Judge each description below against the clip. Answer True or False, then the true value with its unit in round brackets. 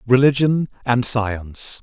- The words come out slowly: True (100 wpm)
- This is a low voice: True (120 Hz)